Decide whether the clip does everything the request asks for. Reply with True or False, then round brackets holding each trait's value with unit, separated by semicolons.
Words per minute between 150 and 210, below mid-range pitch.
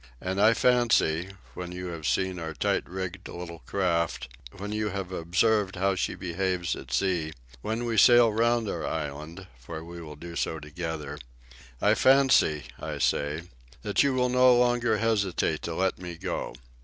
True (170 wpm; 90 Hz)